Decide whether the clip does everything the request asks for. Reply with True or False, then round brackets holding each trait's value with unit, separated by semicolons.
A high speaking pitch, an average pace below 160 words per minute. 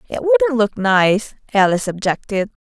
True (230 Hz; 135 wpm)